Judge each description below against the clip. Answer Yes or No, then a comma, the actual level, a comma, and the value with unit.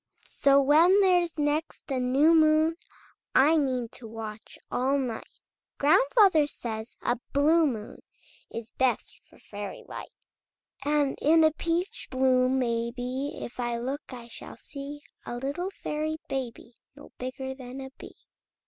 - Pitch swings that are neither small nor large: Yes, average, 3.8 semitones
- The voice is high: Yes, very high, 270 Hz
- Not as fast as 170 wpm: Yes, average, 140 wpm